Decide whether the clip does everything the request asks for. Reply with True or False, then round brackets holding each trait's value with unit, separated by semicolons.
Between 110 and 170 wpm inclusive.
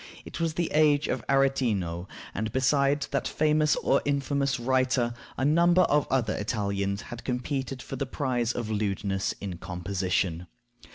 True (150 wpm)